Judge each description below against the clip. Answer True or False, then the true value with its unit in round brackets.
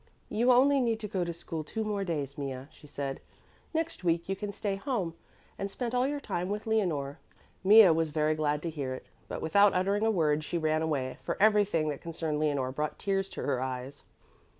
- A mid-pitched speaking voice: True (170 Hz)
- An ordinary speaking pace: False (210 wpm)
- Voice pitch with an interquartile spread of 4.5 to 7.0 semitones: True (5.6 semitones)